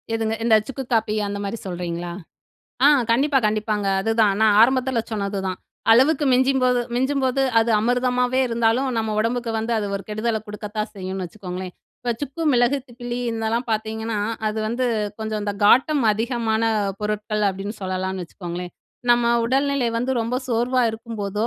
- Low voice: No, high, 225 Hz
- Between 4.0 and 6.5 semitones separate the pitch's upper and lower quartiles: No, average, 2.9 semitones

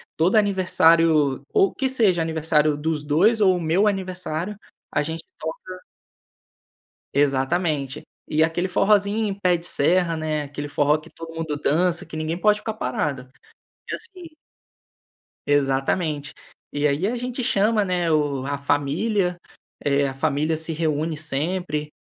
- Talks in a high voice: No, medium, 160 Hz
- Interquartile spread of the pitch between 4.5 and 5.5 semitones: No, average, 4.1 semitones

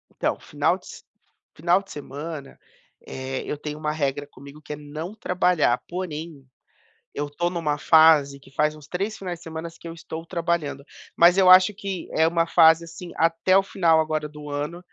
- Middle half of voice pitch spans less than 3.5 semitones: Yes, average, 2.8 semitones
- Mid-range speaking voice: Yes, medium, 160 Hz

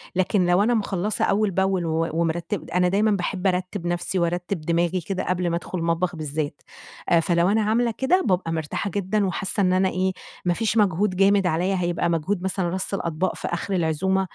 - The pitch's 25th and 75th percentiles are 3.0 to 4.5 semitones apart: No, narrow, 2.5 semitones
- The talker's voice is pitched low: No, medium, 185 Hz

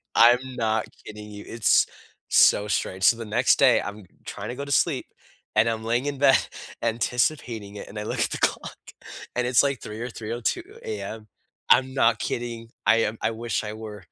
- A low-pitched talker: Yes, low, 115 Hz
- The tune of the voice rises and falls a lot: No, narrow, 2.4 semitones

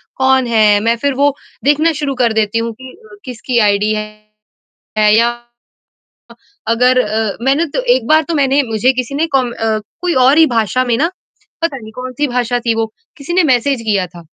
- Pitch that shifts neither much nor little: Yes, average, 3.9 semitones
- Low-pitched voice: No, high, 245 Hz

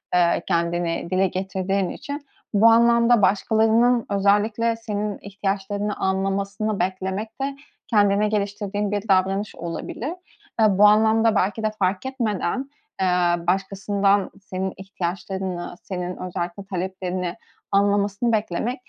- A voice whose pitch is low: No, high, 200 Hz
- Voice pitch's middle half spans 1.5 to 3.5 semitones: Yes, narrow, 2.4 semitones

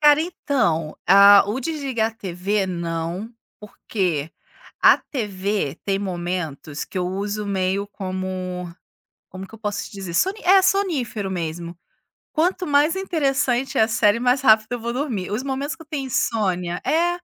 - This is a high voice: Yes, high, 210 Hz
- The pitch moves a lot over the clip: Yes, wide, 6.7 semitones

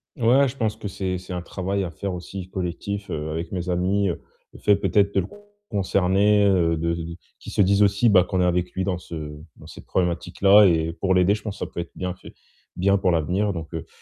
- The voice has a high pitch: No, very low, 95 Hz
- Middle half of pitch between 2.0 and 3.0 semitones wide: Yes, narrow, 2.4 semitones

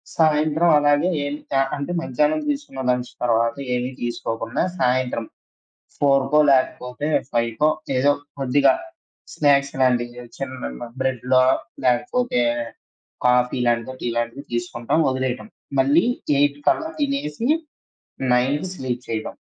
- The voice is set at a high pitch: No, low, 130 Hz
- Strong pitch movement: No, average, 3.1 semitones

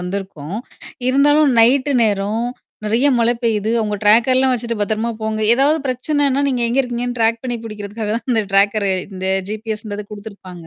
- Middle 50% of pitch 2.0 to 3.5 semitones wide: Yes, average, 3.1 semitones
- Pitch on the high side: Yes, high, 225 Hz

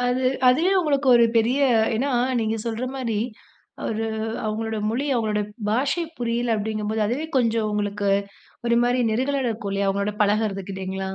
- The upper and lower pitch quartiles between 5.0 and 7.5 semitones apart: No, average, 3.0 semitones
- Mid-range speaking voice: No, high, 225 Hz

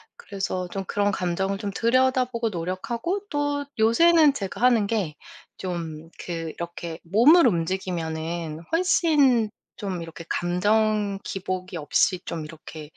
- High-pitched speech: Yes, high, 195 Hz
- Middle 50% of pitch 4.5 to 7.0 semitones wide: Yes, wide, 5.4 semitones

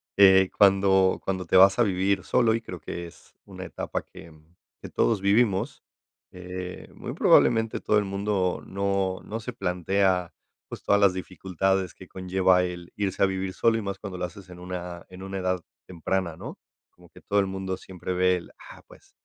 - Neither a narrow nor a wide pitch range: No, narrow, 1.4 semitones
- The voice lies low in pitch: Yes, very low, 95 Hz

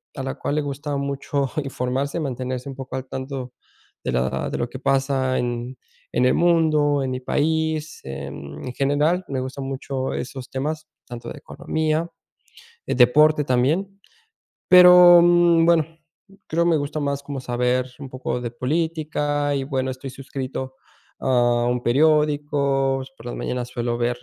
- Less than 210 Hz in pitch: Yes, low, 135 Hz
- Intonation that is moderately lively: Yes, average, 3.1 semitones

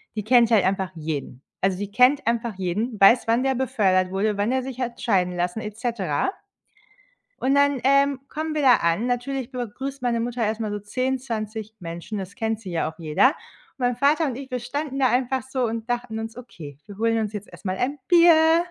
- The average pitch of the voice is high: Yes, high, 235 Hz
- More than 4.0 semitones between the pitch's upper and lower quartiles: Yes, average, 4.5 semitones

